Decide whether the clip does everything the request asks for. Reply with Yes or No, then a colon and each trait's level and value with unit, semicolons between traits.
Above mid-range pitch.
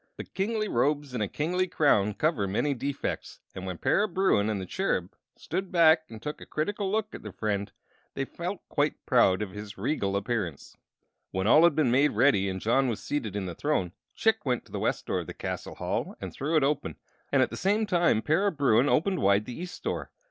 No: medium, 140 Hz